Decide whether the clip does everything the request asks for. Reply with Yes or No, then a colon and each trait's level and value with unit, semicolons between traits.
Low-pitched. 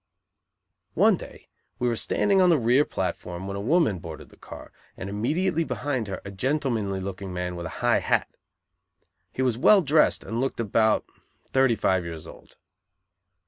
Yes: low, 115 Hz